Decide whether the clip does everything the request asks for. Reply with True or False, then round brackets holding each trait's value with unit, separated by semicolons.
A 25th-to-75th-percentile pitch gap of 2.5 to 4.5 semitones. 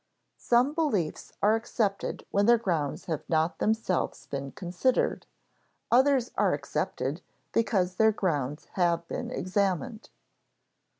False (5.2 semitones)